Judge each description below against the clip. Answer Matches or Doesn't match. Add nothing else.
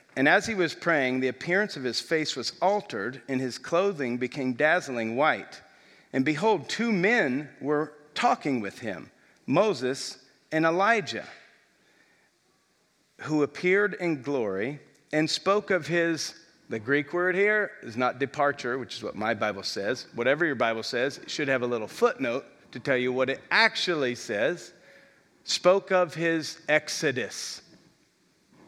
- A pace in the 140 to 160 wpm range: Matches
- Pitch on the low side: Doesn't match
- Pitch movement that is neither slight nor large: Doesn't match